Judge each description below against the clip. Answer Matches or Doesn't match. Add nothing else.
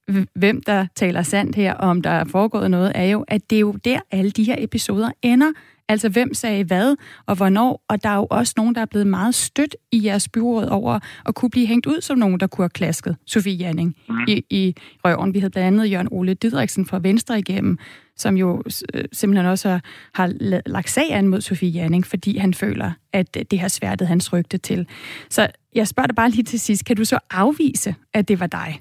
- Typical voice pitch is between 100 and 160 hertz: Doesn't match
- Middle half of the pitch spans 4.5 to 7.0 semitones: Doesn't match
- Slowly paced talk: Doesn't match